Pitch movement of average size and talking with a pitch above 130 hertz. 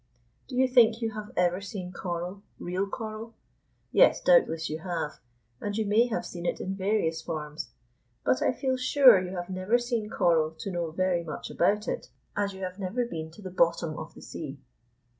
Yes: average, 4.4 semitones; medium, 185 Hz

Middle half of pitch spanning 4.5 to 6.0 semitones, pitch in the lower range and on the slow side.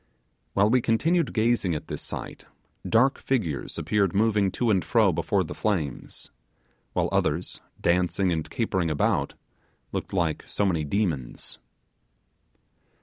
Yes: average, 5.2 semitones; very low, 95 Hz; slow, 130 wpm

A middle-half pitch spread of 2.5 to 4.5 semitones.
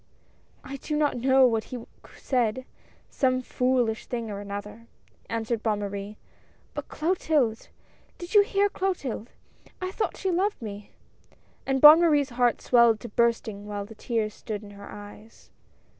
No: average, 4.9 semitones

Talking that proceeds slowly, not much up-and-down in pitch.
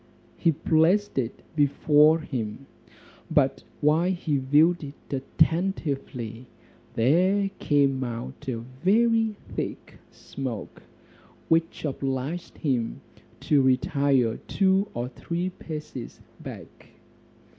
No: slow, 95 wpm; average, 4.7 semitones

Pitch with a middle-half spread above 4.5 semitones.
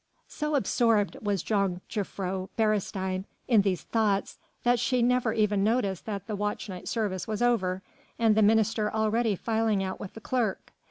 No: narrow, 2.6 semitones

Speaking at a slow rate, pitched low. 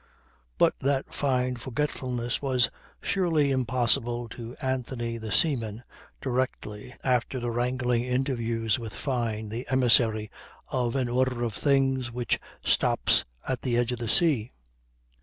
Yes: slow, 130 wpm; low, 125 Hz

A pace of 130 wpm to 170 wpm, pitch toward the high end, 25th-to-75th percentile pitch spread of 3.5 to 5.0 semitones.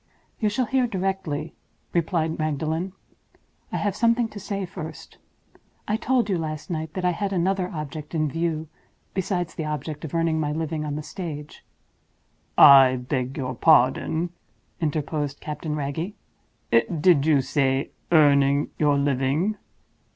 No: average, 145 wpm; medium, 160 Hz; average, 3.8 semitones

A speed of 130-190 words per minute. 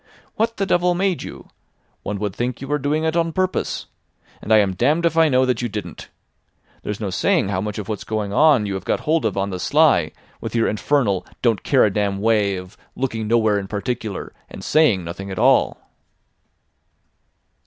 No: average, 200 wpm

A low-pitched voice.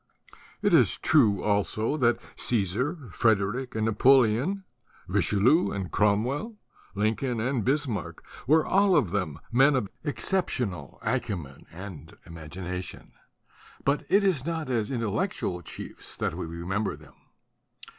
Yes: low, 115 Hz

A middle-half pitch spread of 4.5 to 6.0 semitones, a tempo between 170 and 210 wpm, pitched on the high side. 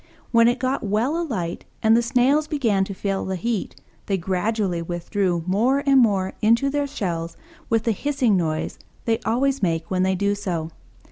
Yes: average, 5.1 semitones; average, 180 wpm; high, 210 Hz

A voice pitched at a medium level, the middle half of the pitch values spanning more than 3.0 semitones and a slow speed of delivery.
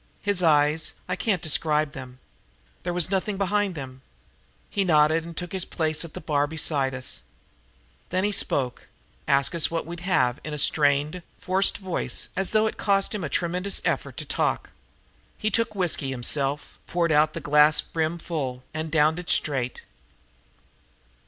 No: medium, 160 Hz; average, 3.8 semitones; average, 165 wpm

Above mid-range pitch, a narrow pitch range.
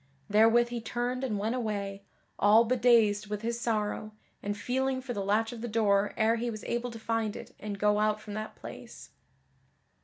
Yes: high, 220 Hz; narrow, 2.3 semitones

